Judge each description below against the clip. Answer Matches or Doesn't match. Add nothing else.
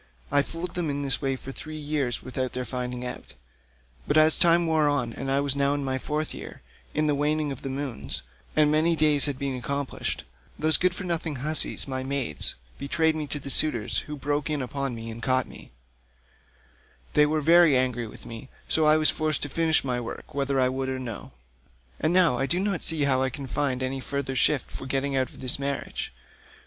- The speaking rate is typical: Doesn't match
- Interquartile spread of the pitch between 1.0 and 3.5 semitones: Matches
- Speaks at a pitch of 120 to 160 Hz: Matches